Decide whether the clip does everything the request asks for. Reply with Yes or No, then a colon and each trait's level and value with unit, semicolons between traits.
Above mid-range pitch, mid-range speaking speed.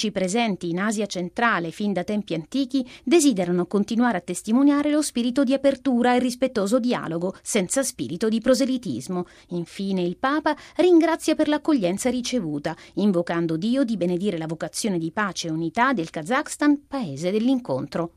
Yes: high, 220 Hz; average, 145 wpm